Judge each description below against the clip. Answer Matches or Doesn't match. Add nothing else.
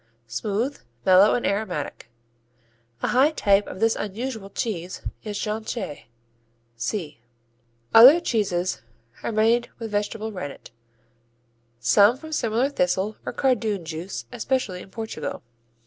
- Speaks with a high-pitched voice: Matches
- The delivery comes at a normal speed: Doesn't match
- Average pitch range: Matches